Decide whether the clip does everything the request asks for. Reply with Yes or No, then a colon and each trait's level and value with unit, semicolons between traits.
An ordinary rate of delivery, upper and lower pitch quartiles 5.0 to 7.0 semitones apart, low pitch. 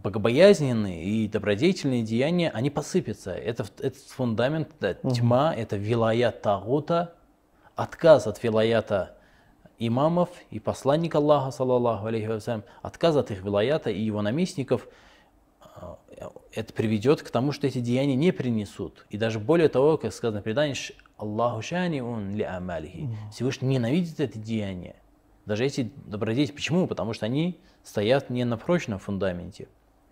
Yes: average, 130 wpm; wide, 5.4 semitones; low, 120 Hz